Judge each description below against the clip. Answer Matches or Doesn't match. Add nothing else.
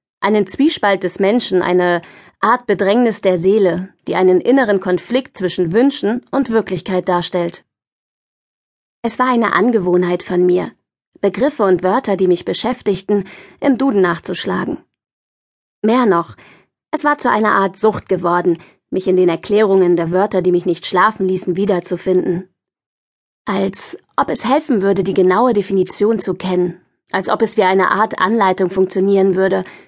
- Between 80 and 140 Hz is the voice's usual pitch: Doesn't match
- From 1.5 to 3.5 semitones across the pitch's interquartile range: Matches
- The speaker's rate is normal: Matches